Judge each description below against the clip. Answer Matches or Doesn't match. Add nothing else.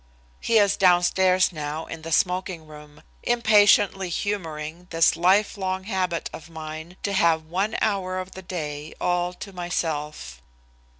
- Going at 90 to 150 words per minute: Matches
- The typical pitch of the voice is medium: Matches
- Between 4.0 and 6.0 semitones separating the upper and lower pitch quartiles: Doesn't match